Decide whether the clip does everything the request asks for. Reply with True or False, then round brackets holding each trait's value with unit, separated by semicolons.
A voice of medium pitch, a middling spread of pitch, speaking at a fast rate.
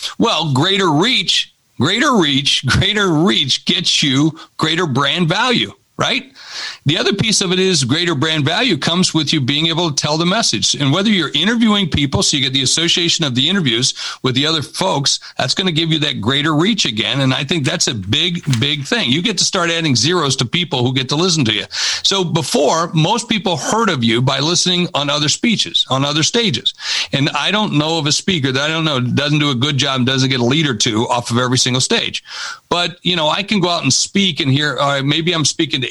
True (155 Hz; 4.6 semitones; 230 wpm)